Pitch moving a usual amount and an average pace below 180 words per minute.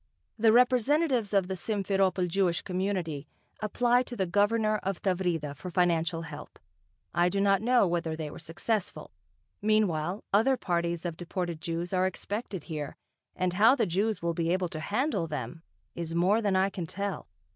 Yes: average, 3.7 semitones; average, 170 wpm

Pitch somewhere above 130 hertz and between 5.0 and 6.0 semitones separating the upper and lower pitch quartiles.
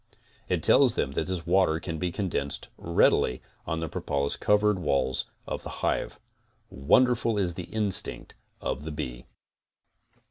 No: very low, 85 Hz; average, 5.3 semitones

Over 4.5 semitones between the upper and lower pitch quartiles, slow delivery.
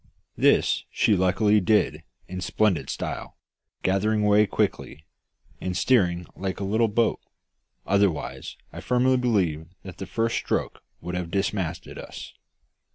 No: average, 3.1 semitones; slow, 130 wpm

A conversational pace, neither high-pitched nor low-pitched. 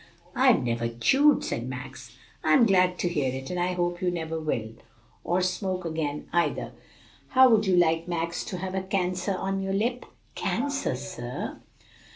Yes: average, 170 wpm; medium, 180 Hz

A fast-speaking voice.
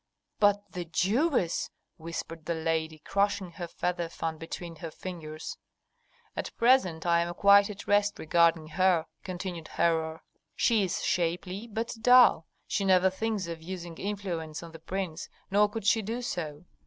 No: average, 155 wpm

